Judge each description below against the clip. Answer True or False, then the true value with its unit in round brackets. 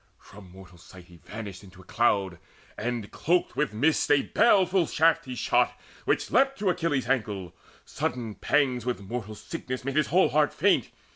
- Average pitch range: False (7.2 semitones)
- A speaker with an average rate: True (165 wpm)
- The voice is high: False (125 Hz)